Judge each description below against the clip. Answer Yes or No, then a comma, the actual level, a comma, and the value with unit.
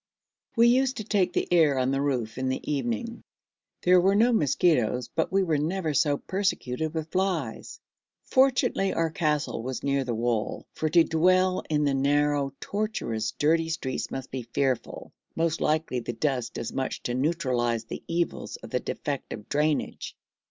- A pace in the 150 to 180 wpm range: Yes, average, 165 wpm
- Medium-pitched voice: Yes, medium, 150 Hz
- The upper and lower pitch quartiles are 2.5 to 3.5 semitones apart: No, average, 5.1 semitones